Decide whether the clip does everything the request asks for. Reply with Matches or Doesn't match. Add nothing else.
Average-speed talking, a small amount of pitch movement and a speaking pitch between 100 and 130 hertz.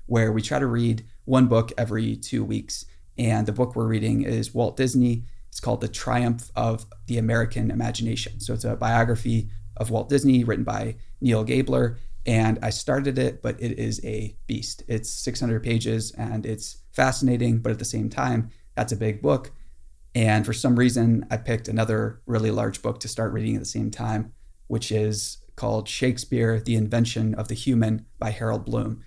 Matches